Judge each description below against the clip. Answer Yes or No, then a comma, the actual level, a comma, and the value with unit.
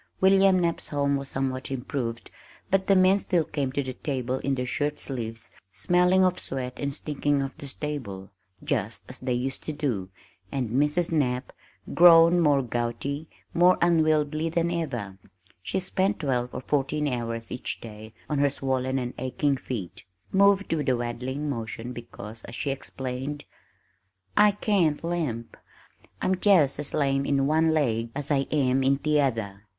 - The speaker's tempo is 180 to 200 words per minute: No, average, 160 wpm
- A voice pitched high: No, medium, 140 Hz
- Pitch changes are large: No, average, 4.1 semitones